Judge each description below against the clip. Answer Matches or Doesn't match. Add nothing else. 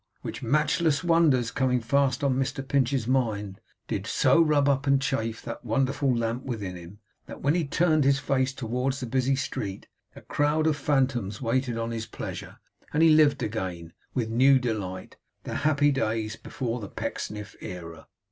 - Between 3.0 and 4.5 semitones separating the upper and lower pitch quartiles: Matches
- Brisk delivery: Doesn't match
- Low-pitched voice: Matches